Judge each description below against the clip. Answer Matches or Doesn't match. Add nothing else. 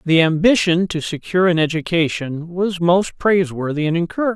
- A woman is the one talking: Doesn't match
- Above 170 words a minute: Doesn't match